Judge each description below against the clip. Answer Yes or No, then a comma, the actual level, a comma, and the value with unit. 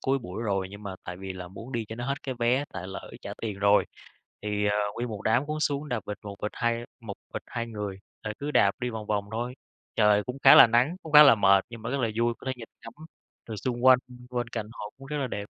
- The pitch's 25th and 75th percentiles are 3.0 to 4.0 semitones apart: Yes, average, 3.5 semitones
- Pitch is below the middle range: Yes, low, 115 Hz